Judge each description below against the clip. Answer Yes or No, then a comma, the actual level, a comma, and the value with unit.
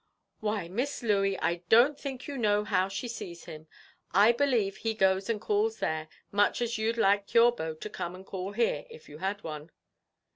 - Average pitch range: Yes, average, 4.1 semitones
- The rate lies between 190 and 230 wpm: Yes, average, 195 wpm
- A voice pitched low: No, high, 205 Hz